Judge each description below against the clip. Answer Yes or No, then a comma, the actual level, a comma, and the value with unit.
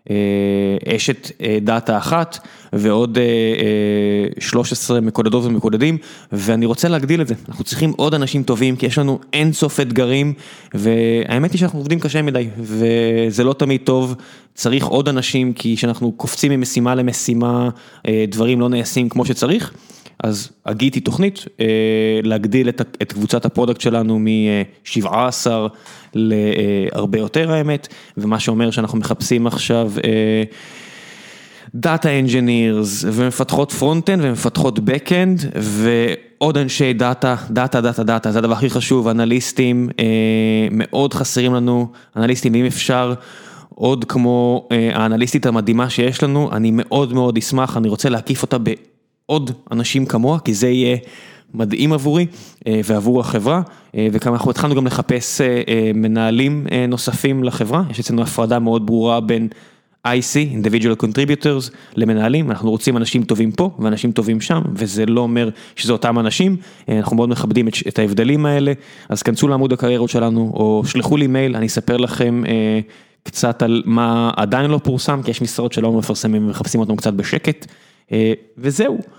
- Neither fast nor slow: Yes, average, 140 wpm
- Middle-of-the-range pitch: No, low, 120 Hz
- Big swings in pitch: No, average, 3.0 semitones